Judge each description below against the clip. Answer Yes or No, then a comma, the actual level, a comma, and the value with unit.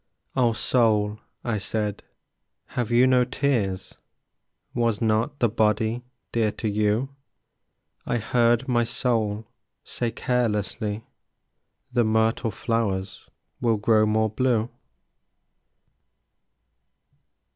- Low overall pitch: Yes, low, 115 Hz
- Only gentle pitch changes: Yes, narrow, 2.2 semitones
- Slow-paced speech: Yes, slow, 95 wpm